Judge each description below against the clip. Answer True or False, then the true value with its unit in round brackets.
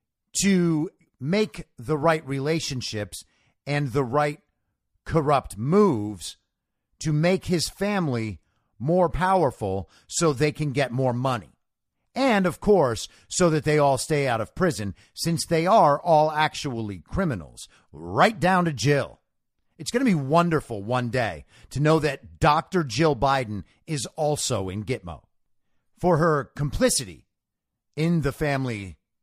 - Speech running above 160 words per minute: False (135 wpm)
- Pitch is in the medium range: True (145 Hz)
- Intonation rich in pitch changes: True (6.4 semitones)